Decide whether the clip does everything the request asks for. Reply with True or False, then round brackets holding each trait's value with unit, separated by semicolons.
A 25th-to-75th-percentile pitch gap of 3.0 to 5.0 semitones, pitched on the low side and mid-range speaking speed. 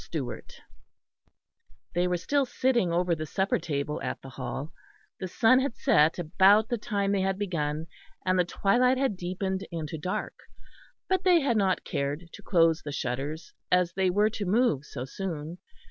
False (4.5 semitones; 180 Hz; 170 wpm)